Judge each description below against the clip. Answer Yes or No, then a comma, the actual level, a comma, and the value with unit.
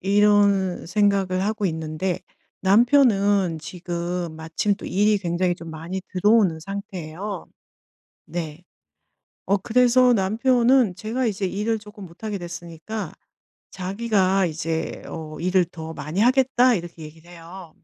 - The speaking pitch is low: No, high, 190 Hz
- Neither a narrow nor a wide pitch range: Yes, average, 3.6 semitones